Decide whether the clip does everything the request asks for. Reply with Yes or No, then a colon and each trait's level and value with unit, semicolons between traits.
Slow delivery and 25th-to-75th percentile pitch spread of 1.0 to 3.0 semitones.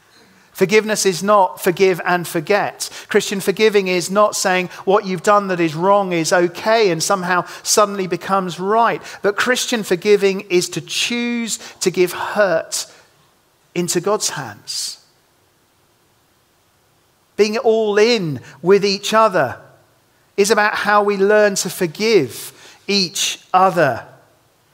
Yes: slow, 125 wpm; narrow, 2.5 semitones